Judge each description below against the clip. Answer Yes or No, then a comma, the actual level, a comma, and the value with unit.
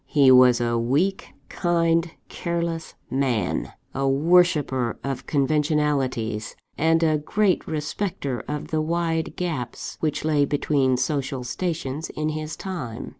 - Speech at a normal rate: No, slow, 125 wpm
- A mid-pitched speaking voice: Yes, medium, 150 Hz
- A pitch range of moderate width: Yes, average, 3.9 semitones